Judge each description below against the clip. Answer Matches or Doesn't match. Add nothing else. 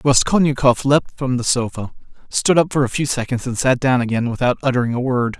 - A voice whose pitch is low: Matches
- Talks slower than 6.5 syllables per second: Matches